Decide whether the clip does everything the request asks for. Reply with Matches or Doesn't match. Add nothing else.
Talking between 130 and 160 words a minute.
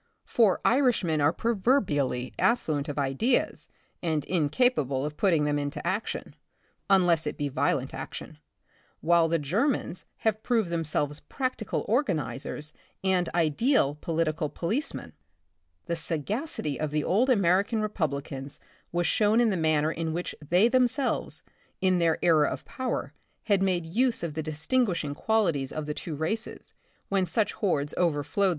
Matches